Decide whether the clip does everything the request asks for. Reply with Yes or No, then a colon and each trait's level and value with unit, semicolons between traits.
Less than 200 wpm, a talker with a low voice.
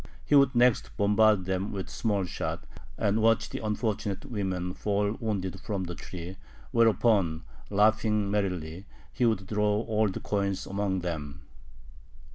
Yes: slow, 135 wpm; low, 100 Hz